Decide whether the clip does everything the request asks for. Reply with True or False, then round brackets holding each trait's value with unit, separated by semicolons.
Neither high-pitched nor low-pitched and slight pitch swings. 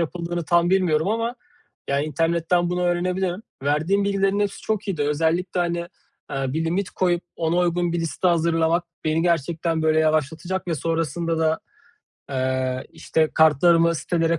True (170 Hz; 2.0 semitones)